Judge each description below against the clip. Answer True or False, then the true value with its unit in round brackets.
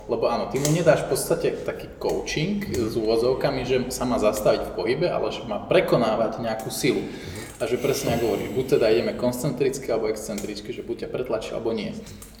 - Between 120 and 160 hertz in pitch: True (130 Hz)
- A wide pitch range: True (7.4 semitones)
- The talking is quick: True (195 wpm)